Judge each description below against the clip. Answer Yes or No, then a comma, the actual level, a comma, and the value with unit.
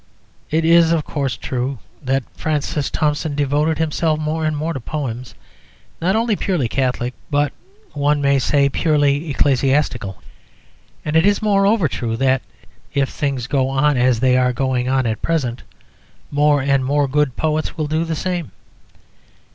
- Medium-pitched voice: Yes, medium, 145 Hz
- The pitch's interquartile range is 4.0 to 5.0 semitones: No, average, 3.1 semitones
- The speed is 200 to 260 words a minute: No, average, 155 wpm